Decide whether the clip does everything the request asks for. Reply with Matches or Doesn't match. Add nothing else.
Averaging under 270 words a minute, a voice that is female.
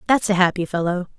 Matches